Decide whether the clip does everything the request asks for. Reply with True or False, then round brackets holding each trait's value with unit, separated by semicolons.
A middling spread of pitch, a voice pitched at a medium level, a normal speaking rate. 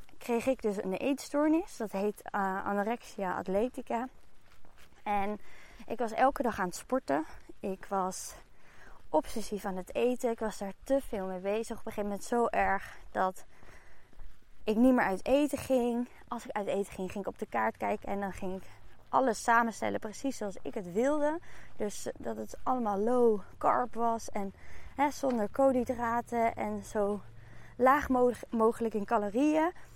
False (4.2 semitones; 225 Hz; 165 wpm)